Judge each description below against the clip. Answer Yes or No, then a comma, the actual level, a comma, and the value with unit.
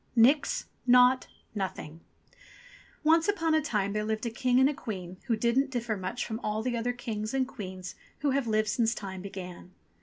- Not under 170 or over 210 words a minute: Yes, average, 185 wpm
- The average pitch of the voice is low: No, high, 230 Hz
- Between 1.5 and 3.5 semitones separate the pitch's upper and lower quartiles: No, average, 4.1 semitones